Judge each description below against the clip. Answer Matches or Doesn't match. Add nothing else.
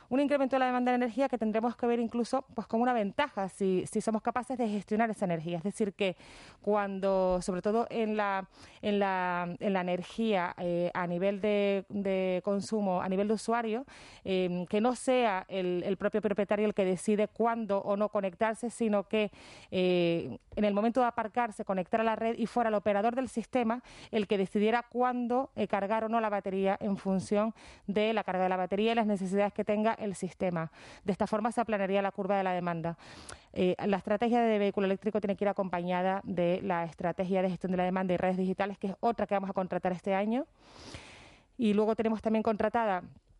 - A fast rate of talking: Matches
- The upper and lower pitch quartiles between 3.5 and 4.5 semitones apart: Doesn't match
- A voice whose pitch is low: Doesn't match